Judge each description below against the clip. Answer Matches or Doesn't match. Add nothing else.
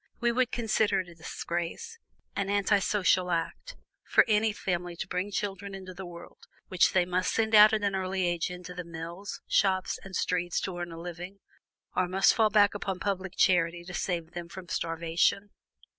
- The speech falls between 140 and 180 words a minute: Doesn't match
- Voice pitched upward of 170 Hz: Matches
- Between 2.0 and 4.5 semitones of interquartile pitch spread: Matches